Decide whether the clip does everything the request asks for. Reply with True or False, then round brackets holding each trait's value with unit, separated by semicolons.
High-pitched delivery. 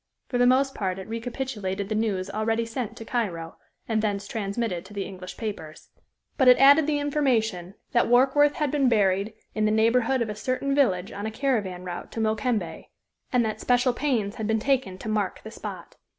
True (220 Hz)